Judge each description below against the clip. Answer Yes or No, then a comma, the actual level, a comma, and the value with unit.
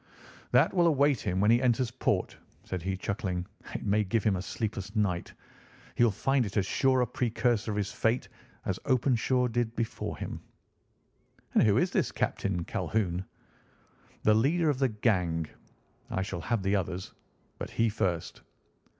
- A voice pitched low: Yes, low, 110 Hz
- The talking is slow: No, average, 165 wpm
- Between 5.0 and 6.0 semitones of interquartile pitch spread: No, average, 4.4 semitones